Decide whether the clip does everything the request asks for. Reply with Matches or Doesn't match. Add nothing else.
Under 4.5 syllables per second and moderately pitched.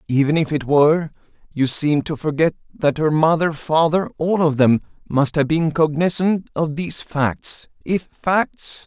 Matches